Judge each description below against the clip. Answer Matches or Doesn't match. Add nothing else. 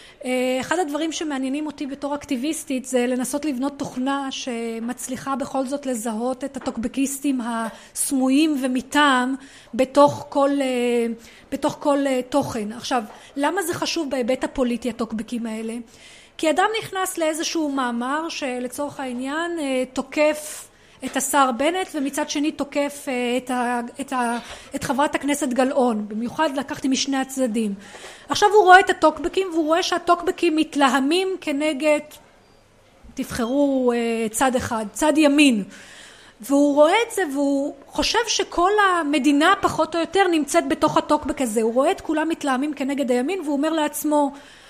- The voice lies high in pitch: Matches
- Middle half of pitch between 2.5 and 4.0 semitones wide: Matches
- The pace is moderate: Matches